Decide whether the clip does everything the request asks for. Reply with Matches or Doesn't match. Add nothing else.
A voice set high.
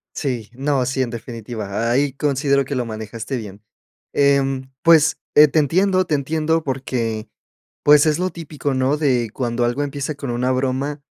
Doesn't match